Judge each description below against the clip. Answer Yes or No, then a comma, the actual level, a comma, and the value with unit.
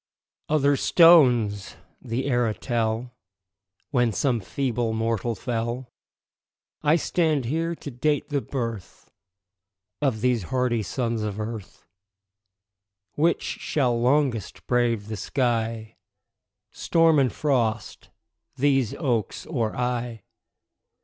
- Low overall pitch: Yes, low, 120 Hz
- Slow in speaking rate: Yes, slow, 105 wpm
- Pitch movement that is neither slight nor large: Yes, average, 3.6 semitones